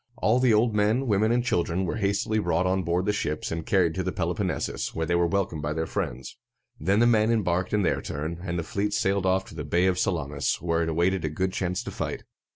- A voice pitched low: Yes, very low, 95 Hz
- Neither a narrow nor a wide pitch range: Yes, average, 3.7 semitones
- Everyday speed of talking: No, fast, 250 wpm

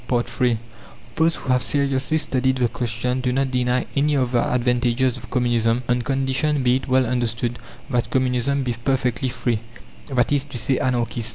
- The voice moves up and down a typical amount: No, narrow, 1.7 semitones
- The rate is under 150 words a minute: No, average, 175 wpm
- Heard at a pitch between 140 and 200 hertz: No, low, 125 Hz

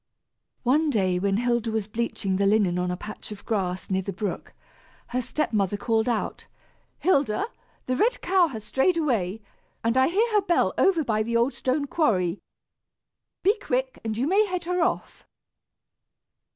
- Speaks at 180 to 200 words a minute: No, average, 170 wpm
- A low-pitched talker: No, high, 235 Hz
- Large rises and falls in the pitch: Yes, wide, 7.2 semitones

